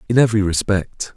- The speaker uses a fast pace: No, average, 155 wpm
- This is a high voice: No, low, 105 Hz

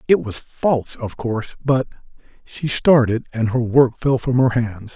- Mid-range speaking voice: No, low, 125 Hz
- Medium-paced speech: Yes, average, 180 wpm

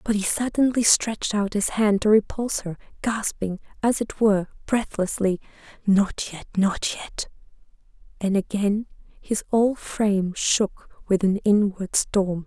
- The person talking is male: No, female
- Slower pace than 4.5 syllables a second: Yes, 4.3 syllables/s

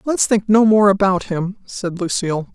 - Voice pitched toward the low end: No, high, 200 Hz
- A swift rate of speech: No, average, 190 wpm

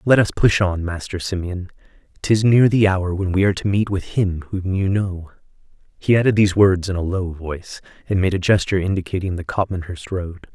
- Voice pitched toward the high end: No, very low, 95 Hz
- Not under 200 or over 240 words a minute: Yes, fast, 205 wpm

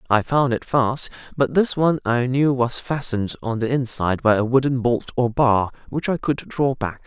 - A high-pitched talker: No, low, 125 Hz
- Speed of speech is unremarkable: No, fast, 210 wpm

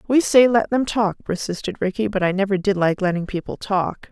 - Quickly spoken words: Yes, fast, 220 wpm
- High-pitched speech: Yes, high, 200 Hz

